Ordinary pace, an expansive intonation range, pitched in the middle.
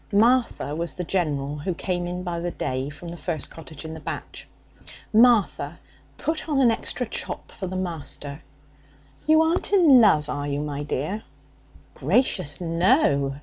Yes: average, 160 wpm; wide, 6.9 semitones; medium, 175 Hz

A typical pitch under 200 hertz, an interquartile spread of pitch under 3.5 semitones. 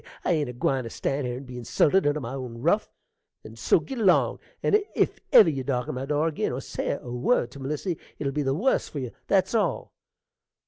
No: medium, 140 Hz; average, 4.8 semitones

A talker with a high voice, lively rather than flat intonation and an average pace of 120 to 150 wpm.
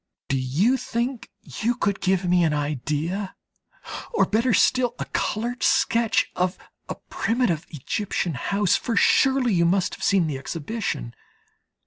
Yes: high, 195 Hz; wide, 6.3 semitones; average, 140 wpm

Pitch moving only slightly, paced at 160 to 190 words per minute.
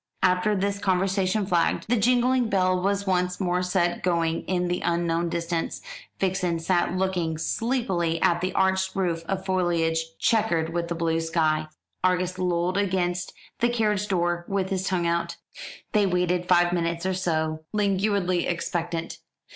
No: narrow, 2.1 semitones; average, 145 wpm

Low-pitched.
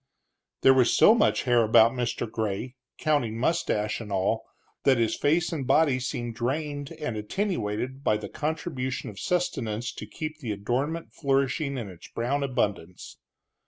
Yes: low, 130 Hz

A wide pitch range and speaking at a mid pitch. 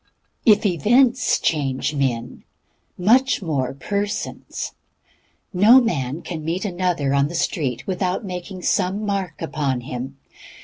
Yes: wide, 6.3 semitones; medium, 175 Hz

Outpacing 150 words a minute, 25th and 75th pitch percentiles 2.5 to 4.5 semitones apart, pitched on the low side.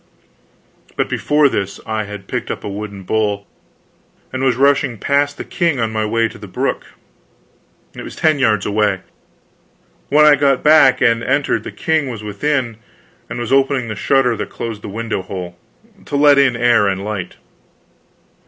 No: average, 170 wpm; average, 4.9 semitones; low, 115 Hz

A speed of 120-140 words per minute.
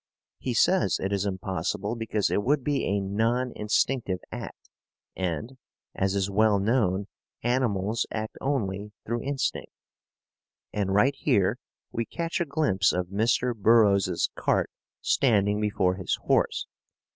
Yes: slow, 135 wpm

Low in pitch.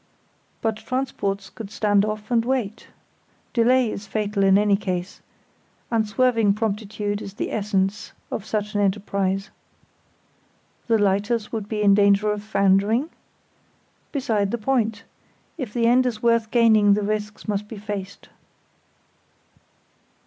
No: high, 210 Hz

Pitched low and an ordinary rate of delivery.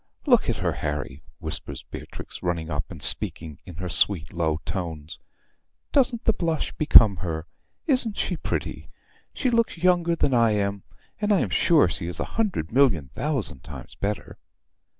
Yes: low, 100 Hz; average, 165 wpm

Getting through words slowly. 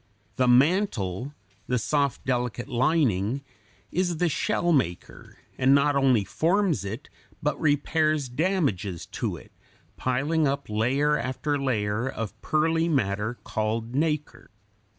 Yes: slow, 120 wpm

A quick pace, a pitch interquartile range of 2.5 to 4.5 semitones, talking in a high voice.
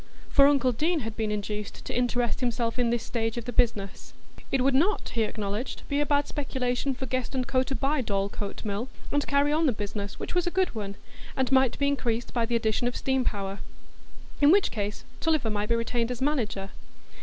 Yes: fast, 215 wpm; average, 4.1 semitones; high, 245 Hz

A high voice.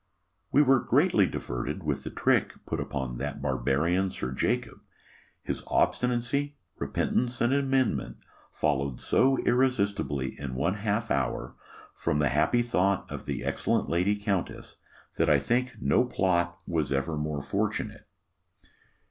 No: very low, 90 Hz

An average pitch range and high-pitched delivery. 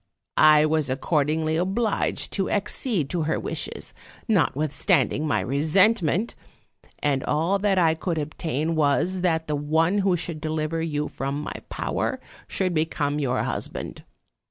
No: average, 3.4 semitones; medium, 160 Hz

